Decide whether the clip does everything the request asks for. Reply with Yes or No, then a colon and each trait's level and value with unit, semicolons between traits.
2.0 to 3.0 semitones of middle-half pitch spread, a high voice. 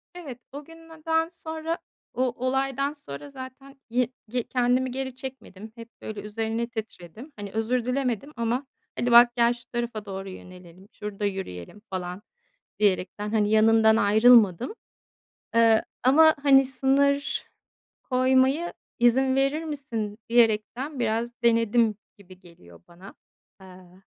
No: average, 4.2 semitones; high, 235 Hz